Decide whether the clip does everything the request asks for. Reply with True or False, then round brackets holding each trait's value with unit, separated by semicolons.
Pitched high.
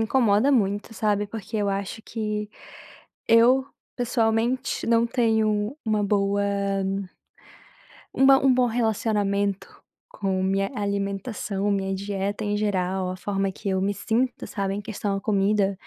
True (205 Hz)